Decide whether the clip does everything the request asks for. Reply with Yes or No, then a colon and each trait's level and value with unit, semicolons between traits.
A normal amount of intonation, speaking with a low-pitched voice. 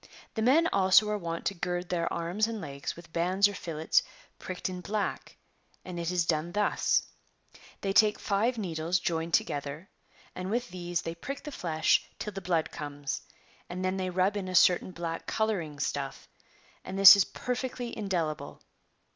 No: average, 3.4 semitones; medium, 180 Hz